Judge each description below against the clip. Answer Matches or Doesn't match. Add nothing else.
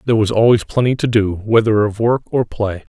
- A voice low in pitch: Matches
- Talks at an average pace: Doesn't match